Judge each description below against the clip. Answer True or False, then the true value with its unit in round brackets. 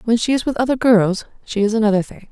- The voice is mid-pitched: False (220 Hz)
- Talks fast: True (260 wpm)